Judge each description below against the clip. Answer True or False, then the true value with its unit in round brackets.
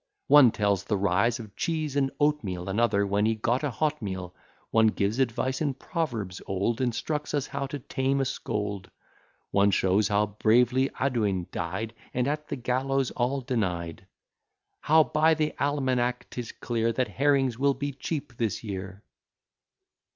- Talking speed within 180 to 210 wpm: False (160 wpm)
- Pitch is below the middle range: True (120 Hz)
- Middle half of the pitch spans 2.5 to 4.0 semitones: False (5.2 semitones)